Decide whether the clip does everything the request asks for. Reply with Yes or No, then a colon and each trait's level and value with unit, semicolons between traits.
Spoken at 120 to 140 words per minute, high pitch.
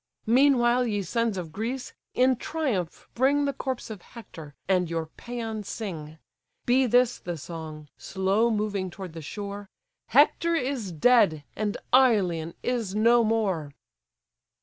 Yes: slow, 135 wpm; high, 215 Hz